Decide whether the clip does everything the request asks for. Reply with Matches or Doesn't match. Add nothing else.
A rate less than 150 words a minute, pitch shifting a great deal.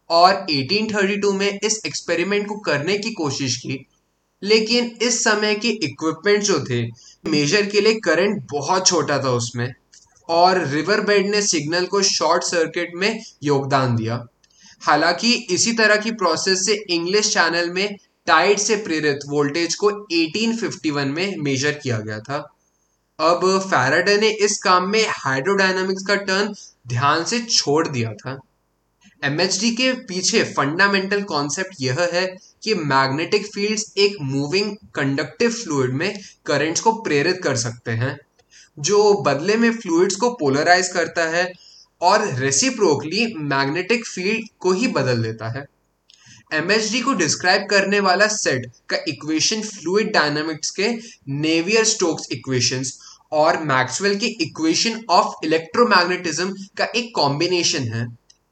Matches